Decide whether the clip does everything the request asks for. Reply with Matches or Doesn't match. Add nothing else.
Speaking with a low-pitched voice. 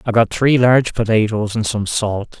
Matches